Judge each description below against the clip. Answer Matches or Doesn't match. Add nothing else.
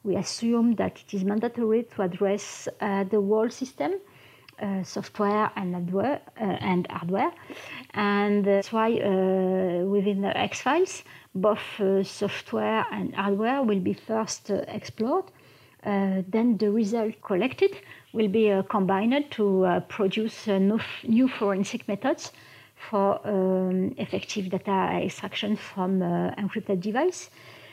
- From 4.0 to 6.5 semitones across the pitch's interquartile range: Doesn't match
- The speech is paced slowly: Matches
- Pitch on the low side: Doesn't match